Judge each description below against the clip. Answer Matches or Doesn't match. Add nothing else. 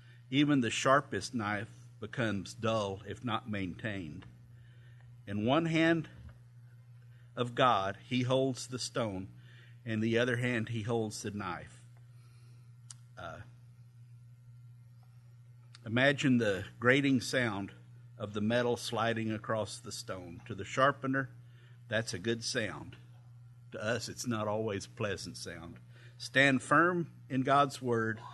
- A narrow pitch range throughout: Matches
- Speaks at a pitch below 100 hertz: Doesn't match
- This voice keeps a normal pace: Doesn't match